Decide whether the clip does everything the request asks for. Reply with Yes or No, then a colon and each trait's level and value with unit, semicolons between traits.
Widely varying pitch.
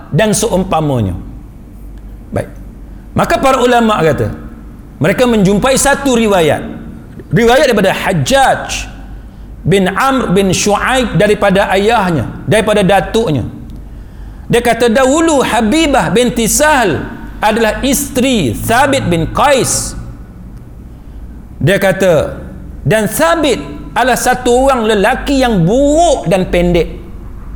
Yes: wide, 8.1 semitones